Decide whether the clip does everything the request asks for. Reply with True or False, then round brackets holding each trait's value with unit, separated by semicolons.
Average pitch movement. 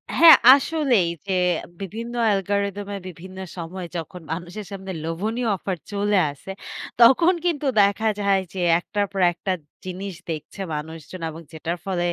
True (3.0 semitones)